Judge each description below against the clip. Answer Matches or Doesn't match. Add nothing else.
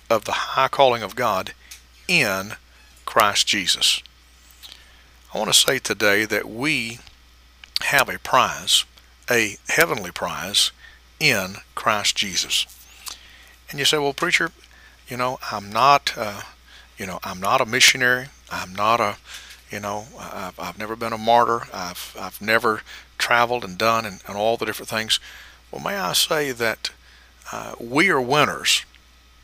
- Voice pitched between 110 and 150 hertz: Doesn't match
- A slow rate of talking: Doesn't match